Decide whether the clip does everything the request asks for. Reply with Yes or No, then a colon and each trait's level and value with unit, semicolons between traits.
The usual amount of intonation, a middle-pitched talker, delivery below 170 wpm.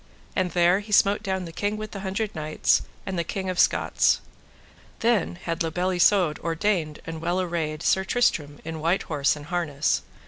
No: average, 3.2 semitones; medium, 175 Hz; average, 185 wpm